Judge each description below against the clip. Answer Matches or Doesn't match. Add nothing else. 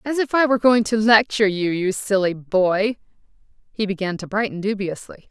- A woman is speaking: Matches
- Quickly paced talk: Doesn't match